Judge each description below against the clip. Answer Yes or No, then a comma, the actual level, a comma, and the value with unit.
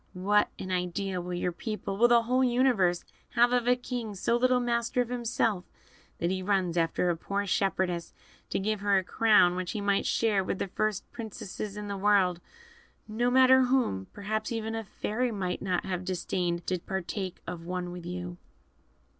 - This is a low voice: No, high, 200 Hz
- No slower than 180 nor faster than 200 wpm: Yes, average, 185 wpm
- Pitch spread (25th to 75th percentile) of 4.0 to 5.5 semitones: Yes, average, 4.3 semitones